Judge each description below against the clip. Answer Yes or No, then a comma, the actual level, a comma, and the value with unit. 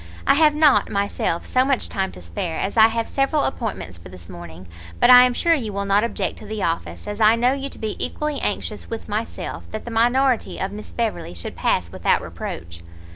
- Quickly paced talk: Yes, fast, 220 wpm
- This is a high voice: Yes, high, 220 Hz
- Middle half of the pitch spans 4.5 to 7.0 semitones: Yes, average, 4.8 semitones